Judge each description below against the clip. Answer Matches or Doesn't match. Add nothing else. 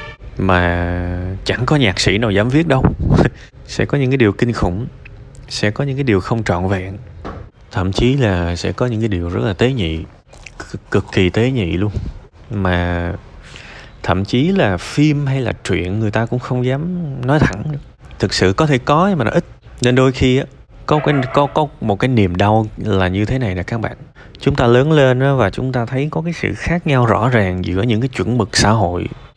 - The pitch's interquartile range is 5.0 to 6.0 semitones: Matches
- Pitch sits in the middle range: Doesn't match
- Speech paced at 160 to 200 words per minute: Doesn't match